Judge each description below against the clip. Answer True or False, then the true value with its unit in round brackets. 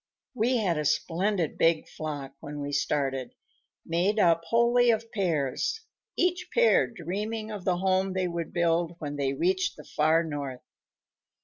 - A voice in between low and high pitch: True (175 Hz)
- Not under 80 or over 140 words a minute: False (150 wpm)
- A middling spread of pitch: False (5.8 semitones)